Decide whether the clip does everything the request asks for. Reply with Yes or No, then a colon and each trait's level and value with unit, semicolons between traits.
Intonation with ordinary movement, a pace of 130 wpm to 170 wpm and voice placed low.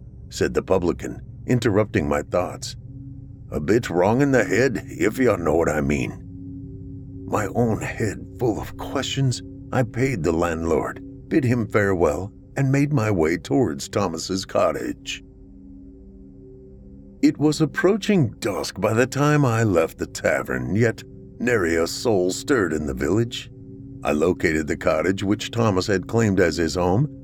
No: wide, 6.3 semitones; average, 150 wpm; low, 110 Hz